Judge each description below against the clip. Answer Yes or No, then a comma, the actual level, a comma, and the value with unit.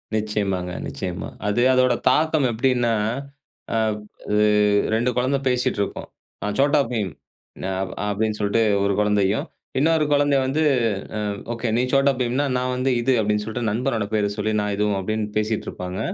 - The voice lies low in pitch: Yes, low, 110 Hz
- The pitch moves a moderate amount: Yes, average, 3.6 semitones